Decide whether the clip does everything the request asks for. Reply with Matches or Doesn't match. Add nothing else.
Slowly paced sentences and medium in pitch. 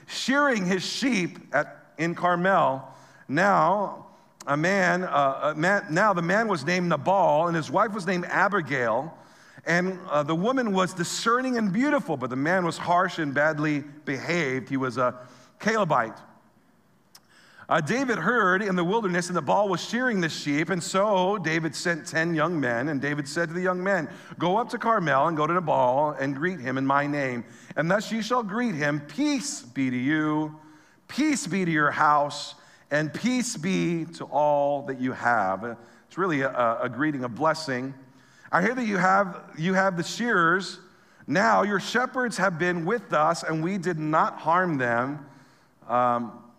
Doesn't match